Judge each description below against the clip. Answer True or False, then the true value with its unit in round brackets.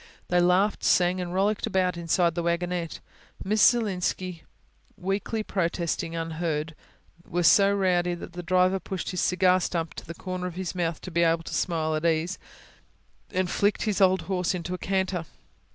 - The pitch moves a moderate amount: False (1.8 semitones)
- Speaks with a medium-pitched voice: True (180 Hz)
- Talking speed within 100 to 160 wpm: False (170 wpm)